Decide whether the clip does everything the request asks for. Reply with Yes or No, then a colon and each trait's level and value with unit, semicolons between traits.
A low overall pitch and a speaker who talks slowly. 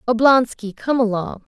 No: high, 235 Hz; slow, 115 wpm